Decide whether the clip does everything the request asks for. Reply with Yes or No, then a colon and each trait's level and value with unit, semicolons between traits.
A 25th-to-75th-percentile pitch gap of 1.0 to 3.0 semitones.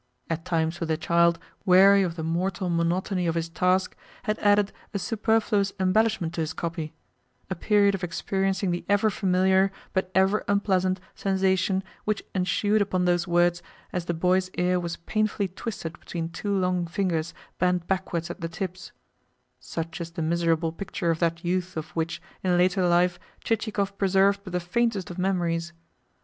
Yes: narrow, 2.4 semitones